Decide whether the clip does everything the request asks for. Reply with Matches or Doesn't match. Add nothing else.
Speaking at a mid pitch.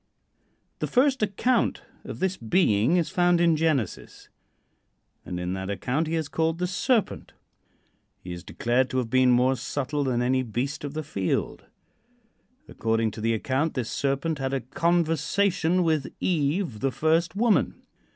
Matches